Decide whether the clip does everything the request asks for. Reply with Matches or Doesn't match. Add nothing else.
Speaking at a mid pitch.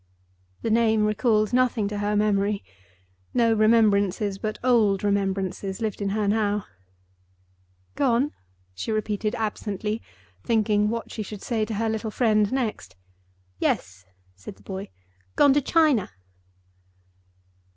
Doesn't match